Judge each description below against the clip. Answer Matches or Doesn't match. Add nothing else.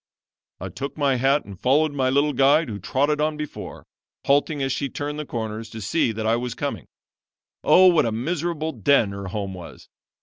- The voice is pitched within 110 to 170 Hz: Matches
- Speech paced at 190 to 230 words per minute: Matches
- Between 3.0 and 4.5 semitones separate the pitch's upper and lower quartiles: Doesn't match